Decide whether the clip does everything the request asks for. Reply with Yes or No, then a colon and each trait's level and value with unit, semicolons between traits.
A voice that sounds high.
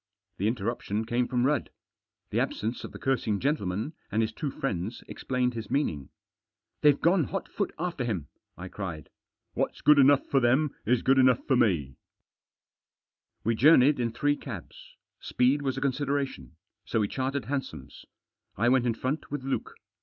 No: low, 125 Hz